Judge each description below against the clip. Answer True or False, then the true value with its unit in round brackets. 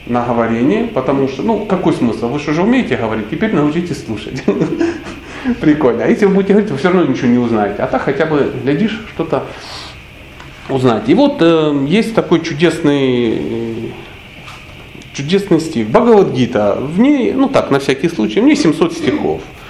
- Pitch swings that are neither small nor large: False (8.8 semitones)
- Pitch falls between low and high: True (160 Hz)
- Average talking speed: False (170 wpm)